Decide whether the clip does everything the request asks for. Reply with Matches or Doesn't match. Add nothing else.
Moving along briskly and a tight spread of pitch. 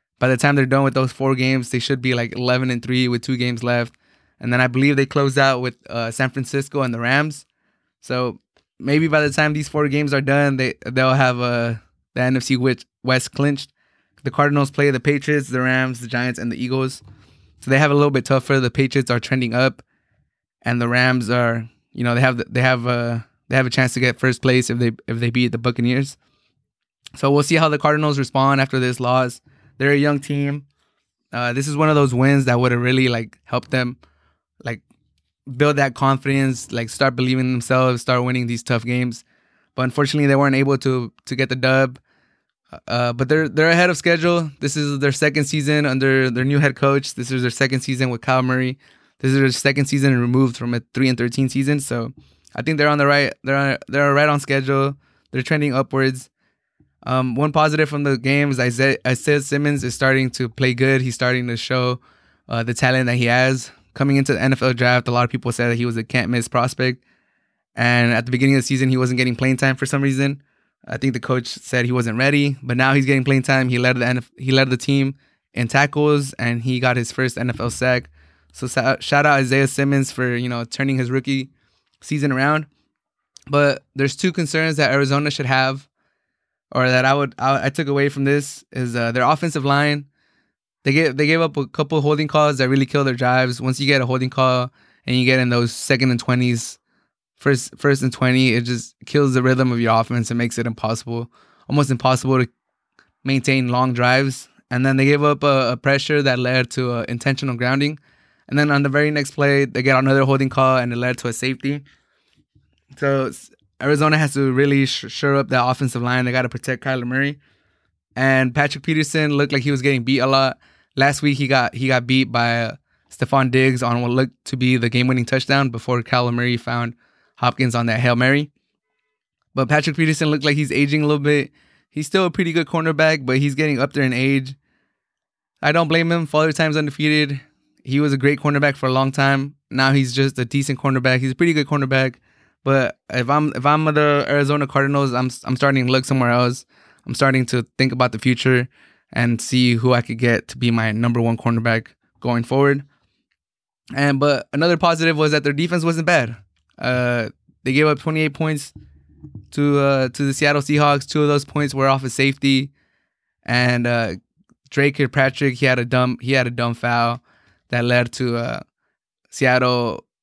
Matches